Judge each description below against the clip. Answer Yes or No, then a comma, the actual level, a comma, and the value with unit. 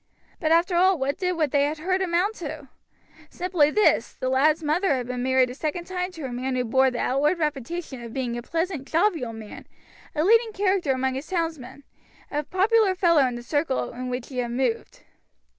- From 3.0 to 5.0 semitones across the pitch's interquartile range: No, wide, 5.5 semitones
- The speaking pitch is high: Yes, very high, 300 Hz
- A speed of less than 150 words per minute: No, average, 200 wpm